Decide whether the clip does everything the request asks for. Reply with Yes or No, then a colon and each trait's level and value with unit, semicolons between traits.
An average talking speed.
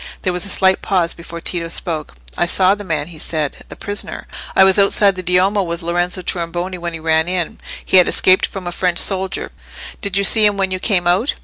No: fast, 220 wpm